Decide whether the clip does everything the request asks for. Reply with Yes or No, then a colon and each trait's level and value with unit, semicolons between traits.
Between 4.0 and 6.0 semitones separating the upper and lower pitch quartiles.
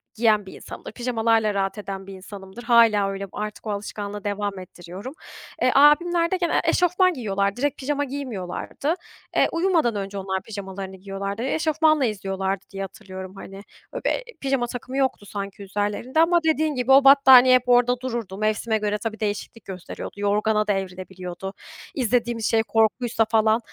Yes: average, 4.5 semitones